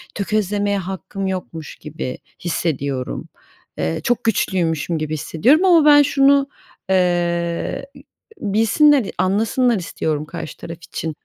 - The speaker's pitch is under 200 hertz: Yes, high, 190 Hz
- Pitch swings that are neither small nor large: No, wide, 5.7 semitones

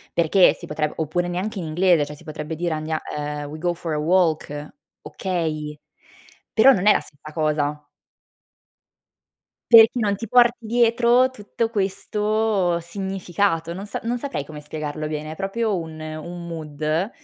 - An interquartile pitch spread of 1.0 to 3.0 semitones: No, average, 5.0 semitones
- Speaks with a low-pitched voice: No, medium, 170 Hz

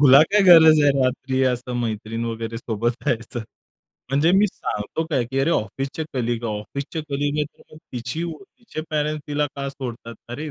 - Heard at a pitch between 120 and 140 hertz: Yes, low, 135 Hz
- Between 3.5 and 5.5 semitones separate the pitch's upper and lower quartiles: Yes, average, 4.4 semitones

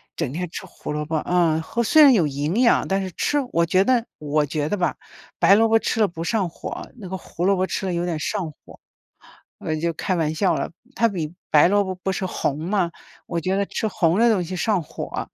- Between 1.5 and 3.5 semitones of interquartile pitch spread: No, average, 3.9 semitones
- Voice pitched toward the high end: No, medium, 180 Hz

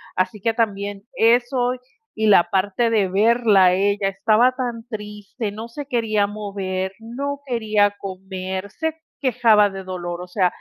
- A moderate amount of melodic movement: Yes, average, 3.2 semitones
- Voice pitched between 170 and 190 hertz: No, high, 210 Hz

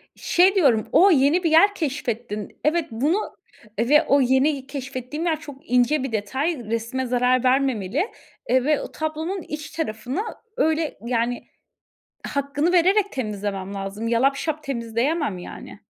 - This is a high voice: Yes, very high, 275 Hz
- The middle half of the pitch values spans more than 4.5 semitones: Yes, average, 4.9 semitones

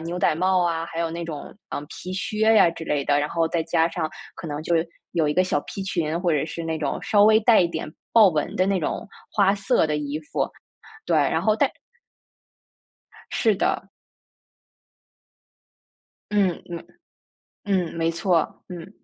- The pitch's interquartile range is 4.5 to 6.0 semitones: No, average, 3.3 semitones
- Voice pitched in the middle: Yes, medium, 170 Hz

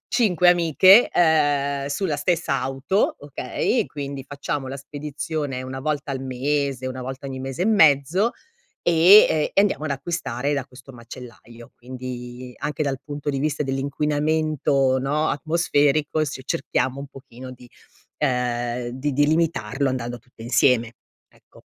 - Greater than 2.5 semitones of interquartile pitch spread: Yes, average, 2.9 semitones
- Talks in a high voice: No, medium, 140 Hz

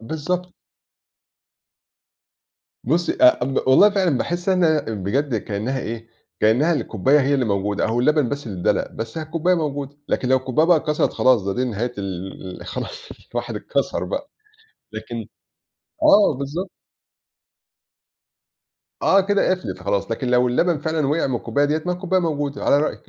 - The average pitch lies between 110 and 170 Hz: Yes, medium, 140 Hz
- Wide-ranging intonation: Yes, wide, 5.9 semitones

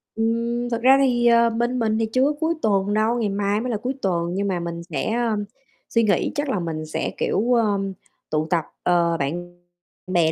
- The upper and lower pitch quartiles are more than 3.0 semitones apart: Yes, average, 5.2 semitones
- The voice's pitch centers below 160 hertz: No, high, 210 Hz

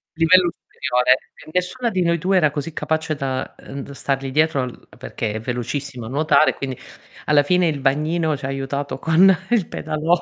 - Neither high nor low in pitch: Yes, medium, 150 Hz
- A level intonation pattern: No, average, 3.6 semitones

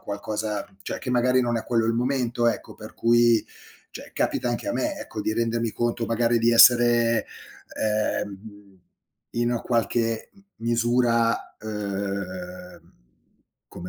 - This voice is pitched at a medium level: No, low, 115 Hz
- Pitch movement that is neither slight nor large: No, narrow, 1.7 semitones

